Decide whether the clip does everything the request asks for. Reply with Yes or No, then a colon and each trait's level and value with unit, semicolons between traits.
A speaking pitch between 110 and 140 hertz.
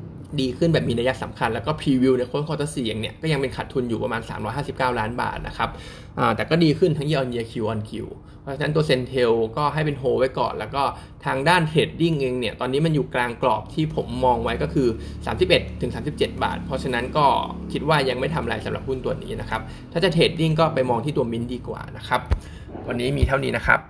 Yes: low, 130 Hz